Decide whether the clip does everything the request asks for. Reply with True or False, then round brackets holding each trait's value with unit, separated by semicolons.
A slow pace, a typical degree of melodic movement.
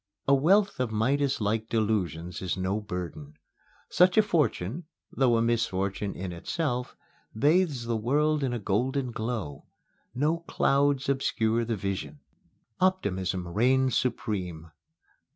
False (120 wpm; 6.1 semitones)